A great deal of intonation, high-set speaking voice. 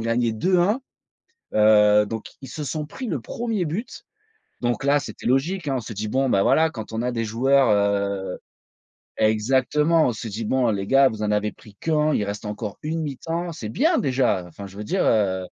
No: wide, 6.2 semitones; low, 120 Hz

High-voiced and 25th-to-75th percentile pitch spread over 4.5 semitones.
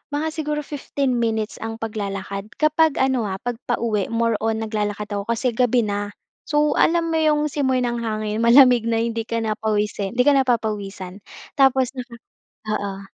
No: high, 230 Hz; average, 3.8 semitones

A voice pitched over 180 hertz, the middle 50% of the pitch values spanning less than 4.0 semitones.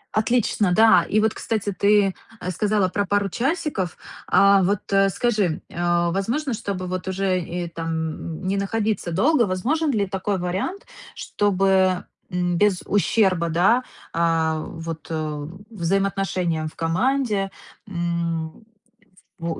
Yes: high, 190 Hz; average, 3.4 semitones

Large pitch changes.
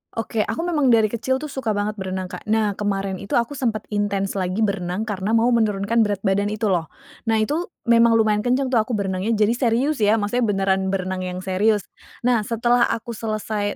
No: average, 2.9 semitones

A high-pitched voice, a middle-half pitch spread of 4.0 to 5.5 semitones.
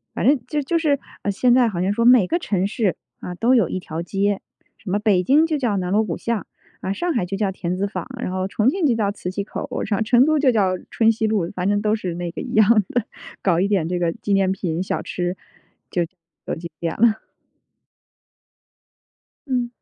Yes: high, 205 Hz; average, 4.4 semitones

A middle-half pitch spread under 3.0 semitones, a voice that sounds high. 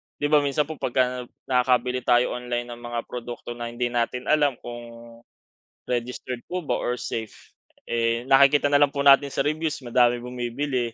No: narrow, 2.6 semitones; low, 125 Hz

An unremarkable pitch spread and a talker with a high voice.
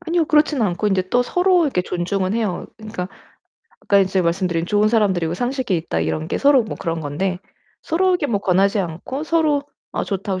No: wide, 7.2 semitones; high, 200 Hz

